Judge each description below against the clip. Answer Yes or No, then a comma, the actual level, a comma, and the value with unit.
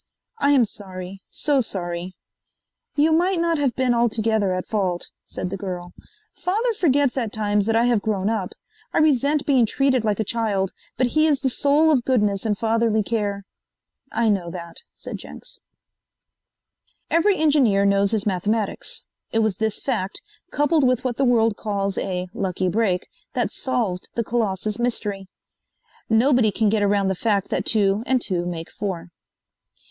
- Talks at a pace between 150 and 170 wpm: Yes, average, 165 wpm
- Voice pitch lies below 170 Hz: No, high, 220 Hz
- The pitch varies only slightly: No, average, 4.7 semitones